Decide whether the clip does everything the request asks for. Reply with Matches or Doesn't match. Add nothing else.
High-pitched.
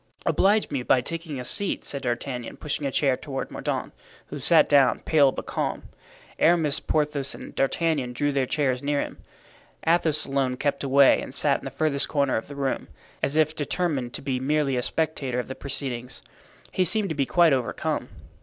Doesn't match